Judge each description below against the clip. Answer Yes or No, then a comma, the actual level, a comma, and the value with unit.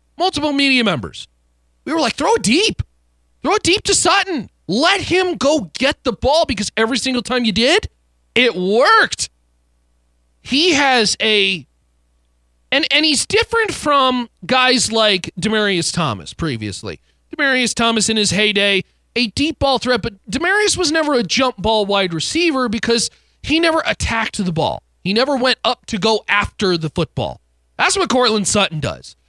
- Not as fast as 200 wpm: Yes, average, 160 wpm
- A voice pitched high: Yes, high, 225 Hz